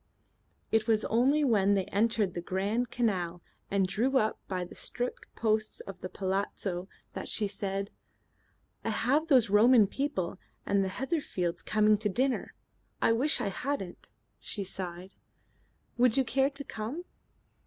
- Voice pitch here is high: Yes, high, 215 Hz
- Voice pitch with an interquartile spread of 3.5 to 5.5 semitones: Yes, average, 4.3 semitones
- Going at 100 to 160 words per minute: Yes, average, 150 wpm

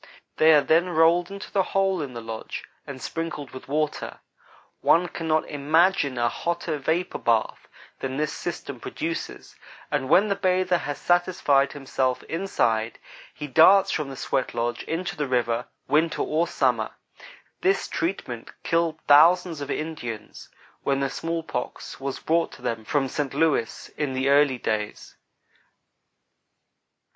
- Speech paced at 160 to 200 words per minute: No, average, 145 wpm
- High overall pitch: No, medium, 150 Hz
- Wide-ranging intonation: No, average, 4.4 semitones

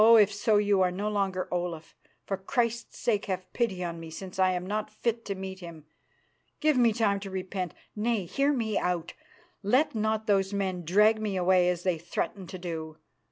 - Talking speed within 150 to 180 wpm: No, average, 195 wpm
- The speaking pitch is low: No, high, 195 Hz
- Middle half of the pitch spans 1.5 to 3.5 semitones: Yes, average, 3.1 semitones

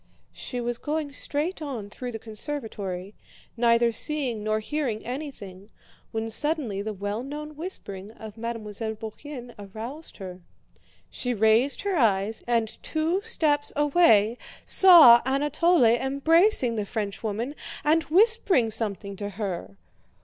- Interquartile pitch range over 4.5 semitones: Yes, wide, 5.6 semitones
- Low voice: No, high, 235 Hz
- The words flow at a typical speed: No, slow, 125 wpm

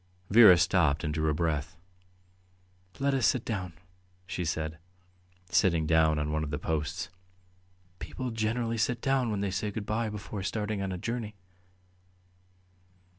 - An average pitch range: No, wide, 5.8 semitones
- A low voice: Yes, very low, 95 Hz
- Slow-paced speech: No, average, 150 wpm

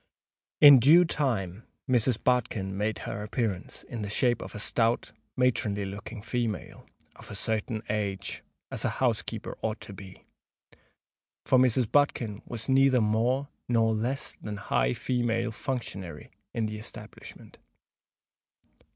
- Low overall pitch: Yes, low, 110 Hz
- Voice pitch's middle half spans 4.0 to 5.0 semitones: No, average, 3.3 semitones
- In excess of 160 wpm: No, slow, 135 wpm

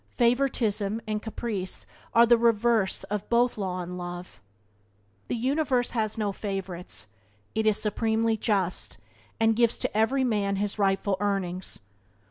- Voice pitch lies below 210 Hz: No, high, 215 Hz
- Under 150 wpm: Yes, slow, 135 wpm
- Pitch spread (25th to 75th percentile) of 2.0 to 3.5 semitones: Yes, average, 3.1 semitones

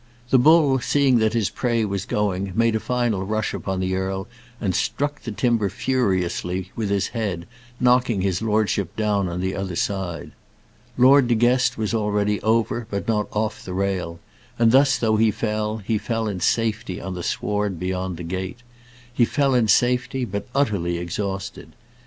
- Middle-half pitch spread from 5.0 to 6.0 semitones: No, average, 3.8 semitones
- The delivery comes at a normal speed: Yes, average, 175 wpm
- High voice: No, low, 105 Hz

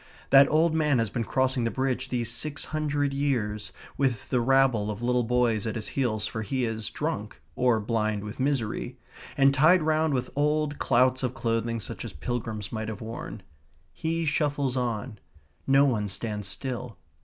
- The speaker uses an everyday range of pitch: Yes, average, 3.8 semitones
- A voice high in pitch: No, low, 125 Hz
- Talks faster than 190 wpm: No, average, 175 wpm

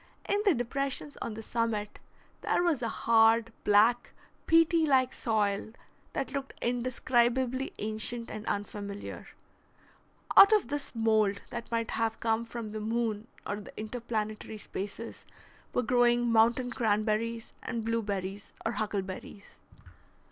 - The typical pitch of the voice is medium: No, high, 230 Hz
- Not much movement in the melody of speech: Yes, narrow, 2.3 semitones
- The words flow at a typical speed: No, slow, 125 wpm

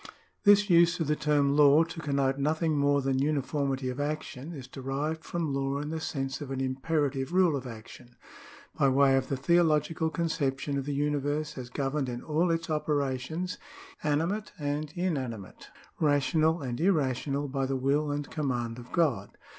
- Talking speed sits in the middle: Yes, average, 170 wpm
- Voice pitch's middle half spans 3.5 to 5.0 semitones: No, average, 2.8 semitones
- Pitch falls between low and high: Yes, medium, 145 Hz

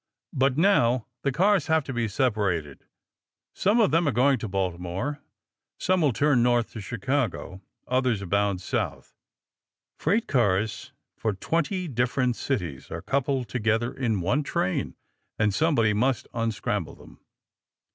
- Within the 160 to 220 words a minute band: No, average, 140 wpm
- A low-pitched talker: Yes, low, 120 Hz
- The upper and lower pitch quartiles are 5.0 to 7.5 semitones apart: Yes, wide, 5.5 semitones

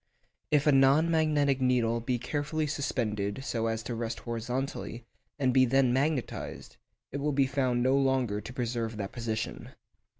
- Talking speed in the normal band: Yes, average, 160 wpm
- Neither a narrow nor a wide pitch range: Yes, average, 3.0 semitones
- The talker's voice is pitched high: No, low, 130 Hz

